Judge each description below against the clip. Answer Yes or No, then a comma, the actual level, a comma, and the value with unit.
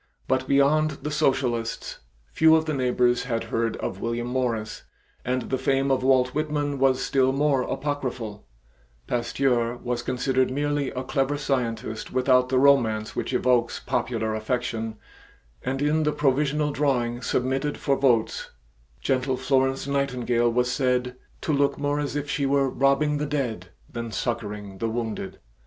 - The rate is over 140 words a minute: Yes, average, 150 wpm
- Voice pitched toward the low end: Yes, low, 130 Hz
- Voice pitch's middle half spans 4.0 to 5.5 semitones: No, average, 2.8 semitones